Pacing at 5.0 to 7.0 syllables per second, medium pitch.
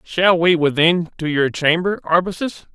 No: 4.4 syllables/s; medium, 170 Hz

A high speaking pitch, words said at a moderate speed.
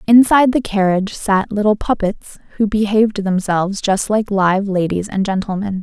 Yes: high, 200 Hz; average, 155 wpm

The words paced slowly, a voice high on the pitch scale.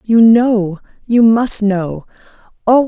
Yes: slow, 85 wpm; high, 220 Hz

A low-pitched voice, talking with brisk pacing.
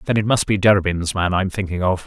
Yes: very low, 95 Hz; fast, 290 wpm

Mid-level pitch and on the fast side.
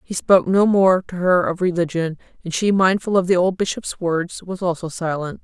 Yes: medium, 180 Hz; fast, 210 wpm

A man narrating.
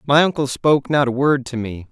Yes: male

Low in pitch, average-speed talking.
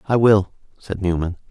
Yes: low, 100 Hz; average, 160 wpm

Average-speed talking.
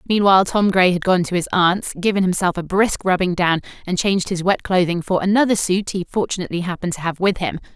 No: fast, 225 wpm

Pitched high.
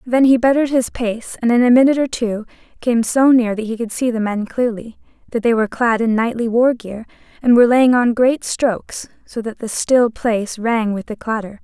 Yes: high, 235 Hz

